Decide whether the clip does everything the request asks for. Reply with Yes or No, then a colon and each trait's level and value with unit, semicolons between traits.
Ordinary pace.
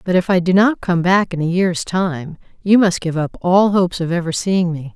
No: fast, 255 wpm